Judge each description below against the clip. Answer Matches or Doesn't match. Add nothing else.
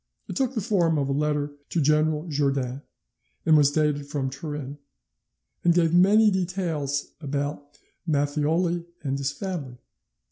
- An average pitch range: Matches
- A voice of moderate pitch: Matches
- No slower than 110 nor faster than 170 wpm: Matches